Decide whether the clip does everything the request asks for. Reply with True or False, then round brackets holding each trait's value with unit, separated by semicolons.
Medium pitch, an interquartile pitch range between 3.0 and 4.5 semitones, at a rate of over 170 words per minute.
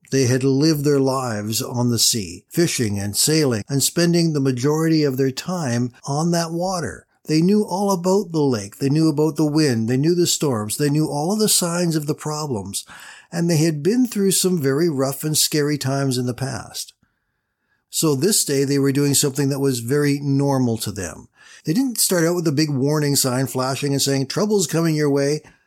True (145 Hz; 3.7 semitones; 205 wpm)